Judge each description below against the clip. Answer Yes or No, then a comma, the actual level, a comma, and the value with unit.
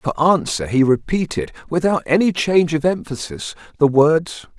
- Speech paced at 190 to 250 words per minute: No, average, 145 wpm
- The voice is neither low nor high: Yes, medium, 155 Hz